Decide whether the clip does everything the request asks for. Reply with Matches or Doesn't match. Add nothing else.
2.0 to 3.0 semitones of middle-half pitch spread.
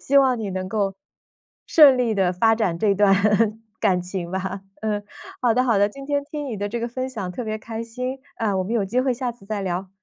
Doesn't match